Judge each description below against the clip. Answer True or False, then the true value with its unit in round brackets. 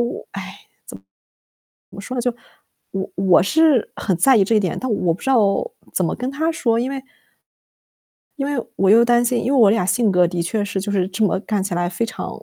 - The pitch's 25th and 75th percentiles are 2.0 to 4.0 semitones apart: False (4.6 semitones)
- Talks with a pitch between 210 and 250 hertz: True (220 Hz)